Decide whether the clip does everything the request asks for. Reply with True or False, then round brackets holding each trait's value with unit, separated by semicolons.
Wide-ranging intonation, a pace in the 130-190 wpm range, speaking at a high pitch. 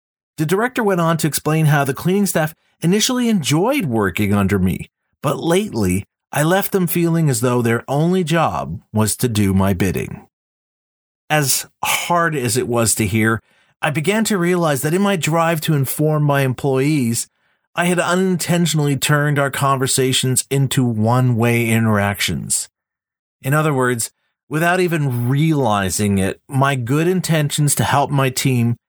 False (5.8 semitones; 155 wpm; 140 Hz)